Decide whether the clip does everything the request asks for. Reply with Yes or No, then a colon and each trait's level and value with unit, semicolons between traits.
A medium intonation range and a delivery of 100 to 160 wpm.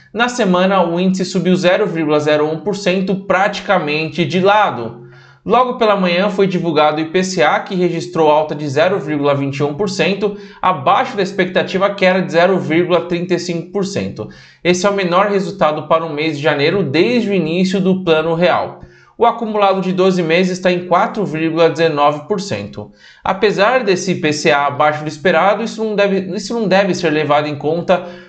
Yes: average, 4.0 semitones; average, 145 wpm